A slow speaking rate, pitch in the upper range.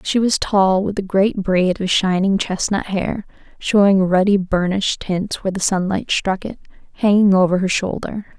No: average, 170 wpm; high, 195 Hz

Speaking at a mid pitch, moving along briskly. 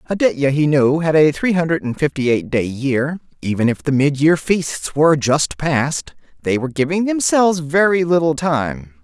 No: medium, 150 Hz; average, 180 wpm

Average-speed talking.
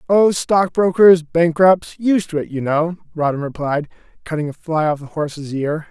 Yes: average, 150 wpm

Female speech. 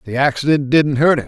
No: male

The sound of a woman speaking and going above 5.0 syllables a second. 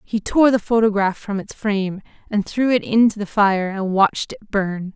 No: female; 4.9 syllables/s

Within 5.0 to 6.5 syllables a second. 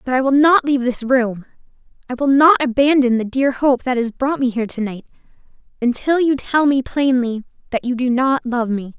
Yes: 5.3 syllables/s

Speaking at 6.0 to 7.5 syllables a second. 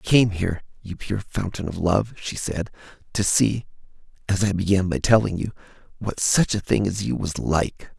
No: 4.9 syllables/s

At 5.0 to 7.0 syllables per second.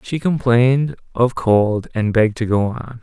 No: 4.5 syllables/s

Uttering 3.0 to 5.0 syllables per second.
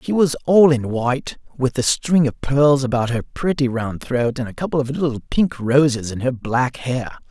Yes: 4.7 syllables/s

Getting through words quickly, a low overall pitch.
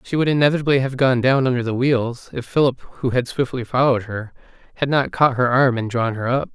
Yes: fast, 230 wpm; low, 130 Hz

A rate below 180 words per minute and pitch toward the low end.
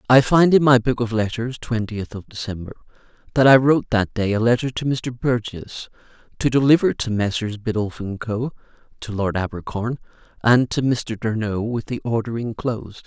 Yes: average, 165 wpm; low, 115 Hz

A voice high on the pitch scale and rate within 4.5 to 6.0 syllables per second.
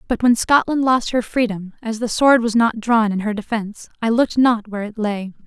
Yes: high, 225 Hz; 5.4 syllables/s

